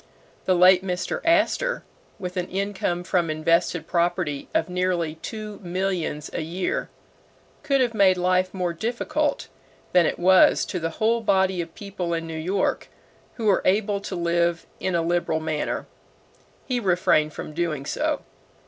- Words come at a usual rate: Yes, average, 155 wpm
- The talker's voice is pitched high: No, medium, 180 Hz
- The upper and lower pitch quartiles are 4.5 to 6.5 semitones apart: No, narrow, 2.6 semitones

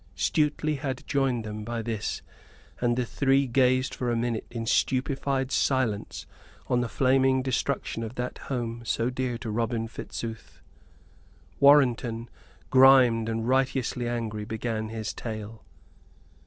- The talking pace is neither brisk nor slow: No, slow, 130 wpm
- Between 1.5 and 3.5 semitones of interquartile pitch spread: Yes, narrow, 2.5 semitones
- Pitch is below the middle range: Yes, low, 120 Hz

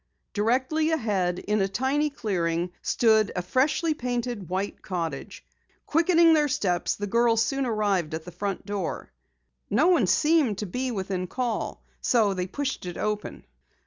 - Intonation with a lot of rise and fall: Yes, wide, 5.9 semitones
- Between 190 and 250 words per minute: No, average, 150 wpm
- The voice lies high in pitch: Yes, high, 215 Hz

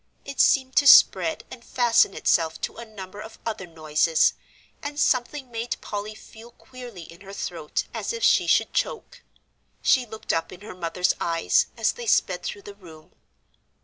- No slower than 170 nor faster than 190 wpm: Yes, average, 175 wpm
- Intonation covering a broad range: Yes, wide, 6.5 semitones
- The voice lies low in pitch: No, high, 215 Hz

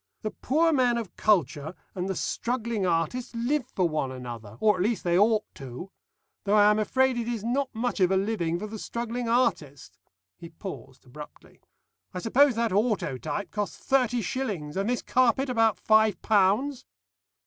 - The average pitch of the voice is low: No, high, 215 Hz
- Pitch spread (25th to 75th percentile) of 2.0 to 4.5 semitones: No, average, 5.2 semitones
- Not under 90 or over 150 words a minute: No, average, 170 wpm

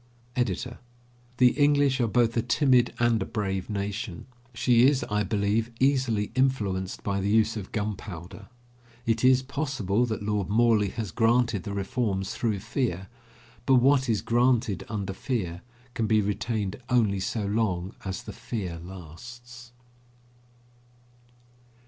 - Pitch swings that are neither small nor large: Yes, average, 3.7 semitones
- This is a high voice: No, low, 110 Hz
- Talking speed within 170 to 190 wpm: No, slow, 135 wpm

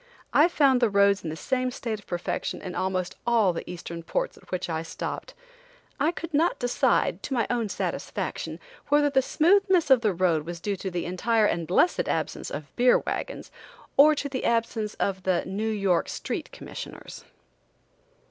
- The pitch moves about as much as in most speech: No, wide, 6.5 semitones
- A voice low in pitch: No, high, 215 Hz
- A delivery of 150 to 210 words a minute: Yes, average, 180 wpm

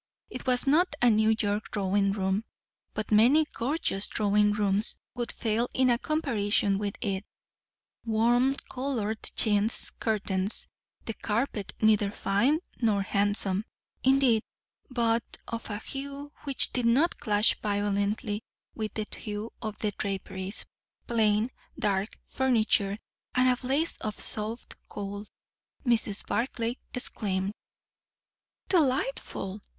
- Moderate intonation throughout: Yes, average, 3.3 semitones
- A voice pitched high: Yes, high, 220 Hz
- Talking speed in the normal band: No, slow, 120 wpm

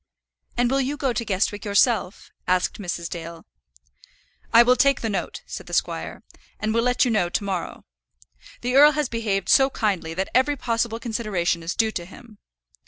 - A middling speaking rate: Yes, average, 180 wpm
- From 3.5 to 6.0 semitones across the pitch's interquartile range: Yes, average, 4.7 semitones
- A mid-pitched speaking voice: No, high, 220 Hz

